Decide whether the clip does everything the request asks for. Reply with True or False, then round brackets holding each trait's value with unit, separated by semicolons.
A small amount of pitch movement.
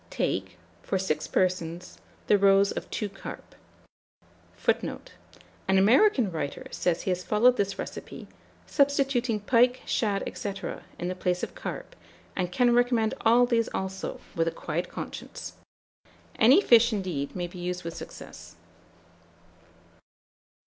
False (4.7 semitones)